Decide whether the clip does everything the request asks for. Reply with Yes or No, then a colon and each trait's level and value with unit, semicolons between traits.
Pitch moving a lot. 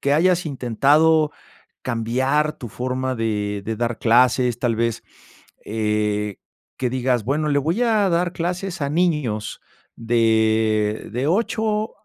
Yes: wide, 5.9 semitones